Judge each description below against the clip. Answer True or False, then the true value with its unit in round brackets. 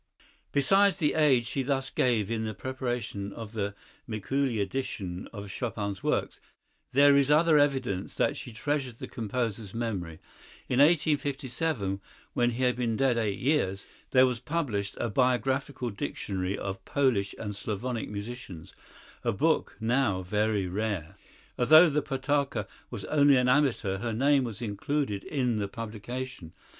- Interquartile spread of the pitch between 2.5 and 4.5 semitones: False (4.9 semitones)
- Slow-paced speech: False (145 wpm)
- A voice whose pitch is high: False (120 Hz)